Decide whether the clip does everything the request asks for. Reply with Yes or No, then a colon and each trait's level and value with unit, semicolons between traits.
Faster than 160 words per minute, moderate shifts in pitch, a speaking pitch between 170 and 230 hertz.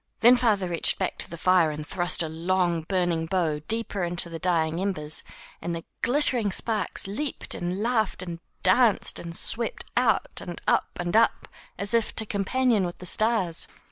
Yes: average, 175 wpm; average, 4.6 semitones; medium, 185 Hz